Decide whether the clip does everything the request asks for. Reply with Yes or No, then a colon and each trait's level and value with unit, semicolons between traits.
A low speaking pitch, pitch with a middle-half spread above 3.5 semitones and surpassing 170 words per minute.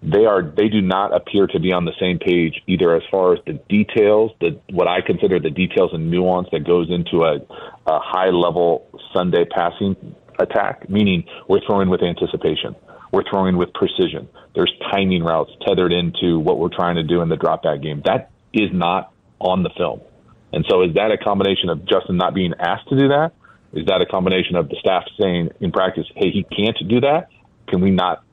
No: very low, 90 Hz; average, 2.7 semitones; fast, 205 wpm